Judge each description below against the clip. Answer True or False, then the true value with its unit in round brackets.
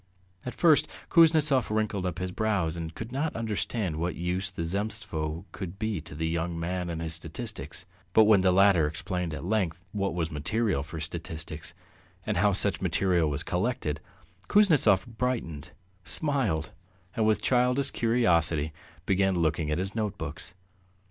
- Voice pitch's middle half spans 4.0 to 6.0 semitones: True (5.1 semitones)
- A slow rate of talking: False (155 wpm)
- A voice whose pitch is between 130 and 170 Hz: False (95 Hz)